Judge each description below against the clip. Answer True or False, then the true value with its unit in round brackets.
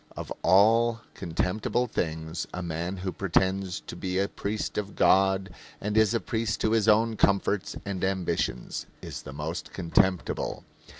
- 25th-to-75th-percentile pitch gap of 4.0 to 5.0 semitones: False (3.0 semitones)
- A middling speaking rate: True (155 wpm)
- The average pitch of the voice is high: False (95 Hz)